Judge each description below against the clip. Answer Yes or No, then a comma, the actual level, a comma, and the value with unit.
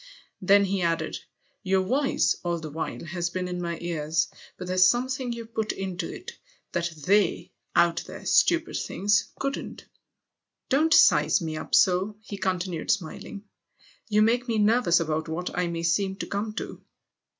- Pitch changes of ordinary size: Yes, average, 3.8 semitones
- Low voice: No, medium, 185 Hz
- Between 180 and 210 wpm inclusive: No, average, 165 wpm